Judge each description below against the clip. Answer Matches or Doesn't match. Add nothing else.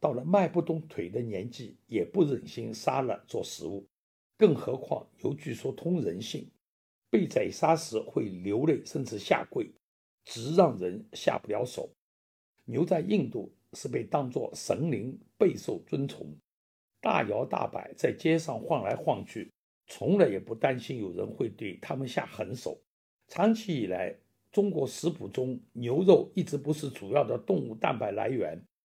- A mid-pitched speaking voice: Matches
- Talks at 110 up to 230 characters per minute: Matches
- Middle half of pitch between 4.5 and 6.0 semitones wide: Doesn't match